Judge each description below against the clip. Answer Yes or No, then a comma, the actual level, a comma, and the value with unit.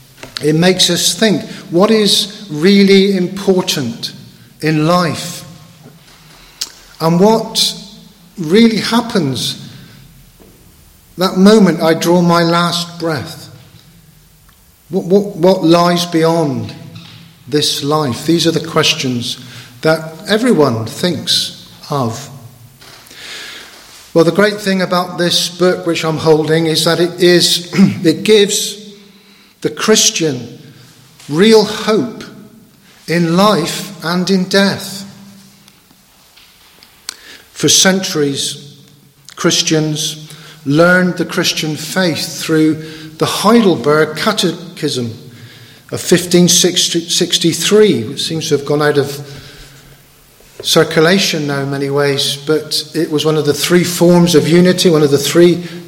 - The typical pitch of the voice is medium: Yes, medium, 165 Hz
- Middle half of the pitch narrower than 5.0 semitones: Yes, average, 3.8 semitones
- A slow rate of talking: Yes, slow, 110 wpm